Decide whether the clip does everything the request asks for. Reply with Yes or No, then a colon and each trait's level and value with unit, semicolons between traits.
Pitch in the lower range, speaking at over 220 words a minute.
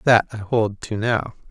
No: low, 110 Hz; average, 200 wpm